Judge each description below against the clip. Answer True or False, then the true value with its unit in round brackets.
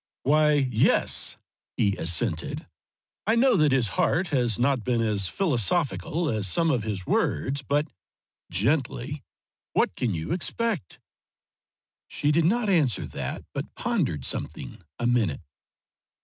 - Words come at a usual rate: False (130 wpm)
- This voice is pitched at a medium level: False (130 Hz)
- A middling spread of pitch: False (6.5 semitones)